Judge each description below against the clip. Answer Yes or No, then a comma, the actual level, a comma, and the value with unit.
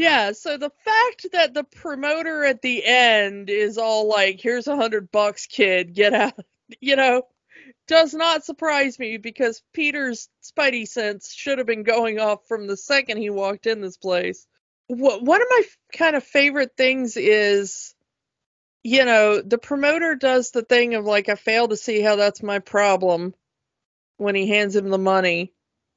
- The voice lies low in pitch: No, high, 230 Hz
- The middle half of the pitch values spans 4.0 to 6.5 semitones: Yes, average, 5.2 semitones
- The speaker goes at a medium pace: Yes, average, 170 wpm